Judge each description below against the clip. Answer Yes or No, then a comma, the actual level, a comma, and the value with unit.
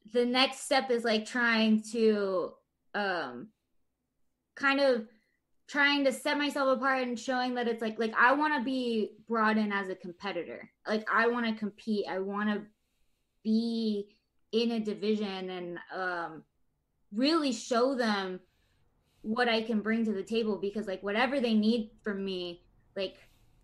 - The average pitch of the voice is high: Yes, high, 220 Hz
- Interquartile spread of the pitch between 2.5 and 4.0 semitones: Yes, average, 3.1 semitones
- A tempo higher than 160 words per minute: No, average, 155 wpm